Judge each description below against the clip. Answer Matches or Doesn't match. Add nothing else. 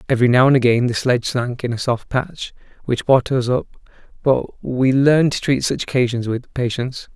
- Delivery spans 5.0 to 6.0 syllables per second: Matches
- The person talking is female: Doesn't match